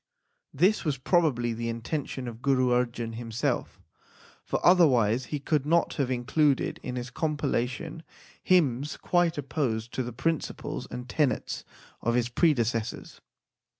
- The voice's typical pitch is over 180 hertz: No, low, 130 Hz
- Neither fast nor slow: No, slow, 130 wpm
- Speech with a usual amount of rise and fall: Yes, average, 4.3 semitones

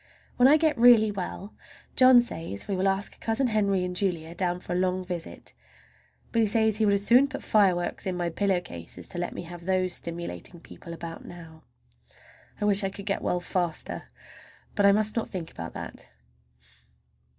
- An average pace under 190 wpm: No, average, 195 wpm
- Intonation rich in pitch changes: No, average, 3.5 semitones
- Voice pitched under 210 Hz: Yes, high, 190 Hz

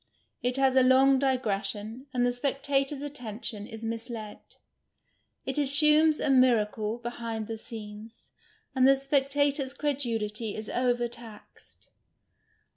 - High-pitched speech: Yes, high, 245 Hz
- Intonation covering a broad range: No, average, 3.5 semitones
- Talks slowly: Yes, slow, 120 wpm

